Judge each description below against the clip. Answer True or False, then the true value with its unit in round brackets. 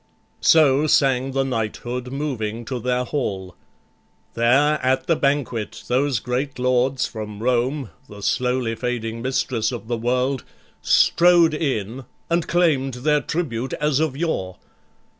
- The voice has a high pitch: False (130 Hz)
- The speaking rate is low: True (130 wpm)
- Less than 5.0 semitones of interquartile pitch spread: True (3.2 semitones)